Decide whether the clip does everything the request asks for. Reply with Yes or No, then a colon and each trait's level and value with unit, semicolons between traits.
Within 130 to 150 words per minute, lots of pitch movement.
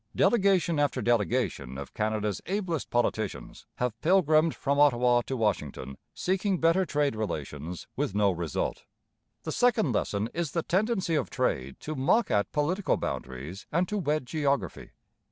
Yes: average, 145 wpm; wide, 8.6 semitones